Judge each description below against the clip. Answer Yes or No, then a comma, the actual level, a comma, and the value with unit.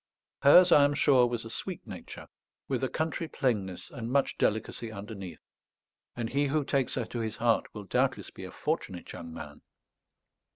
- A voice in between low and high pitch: No, low, 120 Hz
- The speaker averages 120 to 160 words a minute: No, average, 175 wpm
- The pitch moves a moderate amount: Yes, average, 4.9 semitones